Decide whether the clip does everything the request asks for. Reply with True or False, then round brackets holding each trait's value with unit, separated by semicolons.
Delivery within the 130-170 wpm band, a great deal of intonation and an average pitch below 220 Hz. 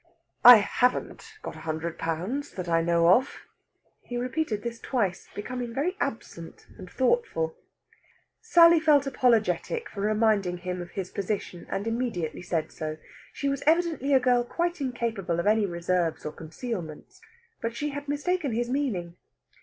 False (155 wpm; 7.7 semitones; 225 Hz)